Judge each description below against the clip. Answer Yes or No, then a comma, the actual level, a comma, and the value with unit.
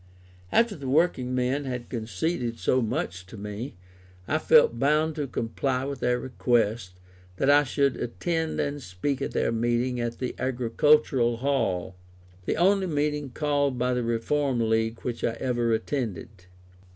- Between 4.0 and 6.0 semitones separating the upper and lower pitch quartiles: No, average, 3.6 semitones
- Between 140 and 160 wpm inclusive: Yes, average, 150 wpm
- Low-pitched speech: Yes, low, 125 Hz